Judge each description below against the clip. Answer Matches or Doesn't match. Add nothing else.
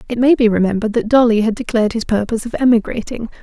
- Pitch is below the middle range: Doesn't match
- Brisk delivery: Matches